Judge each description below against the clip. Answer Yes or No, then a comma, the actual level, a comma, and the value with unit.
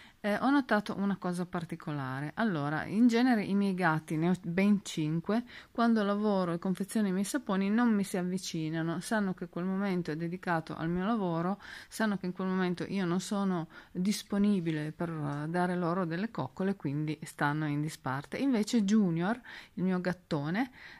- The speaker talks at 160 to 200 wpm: Yes, fast, 170 wpm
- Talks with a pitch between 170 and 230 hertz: Yes, medium, 185 Hz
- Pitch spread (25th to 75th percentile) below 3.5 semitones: No, average, 3.8 semitones